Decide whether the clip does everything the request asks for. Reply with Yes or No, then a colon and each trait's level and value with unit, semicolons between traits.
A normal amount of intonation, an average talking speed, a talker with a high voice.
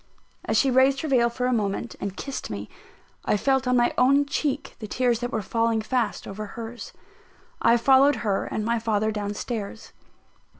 Yes: average, 3.4 semitones; average, 185 wpm; high, 235 Hz